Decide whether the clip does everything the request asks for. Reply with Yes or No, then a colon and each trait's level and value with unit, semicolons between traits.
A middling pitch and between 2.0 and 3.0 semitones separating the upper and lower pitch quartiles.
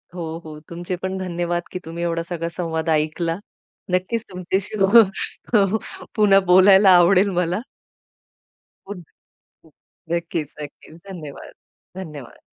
Yes: medium, 175 Hz; narrow, 2.4 semitones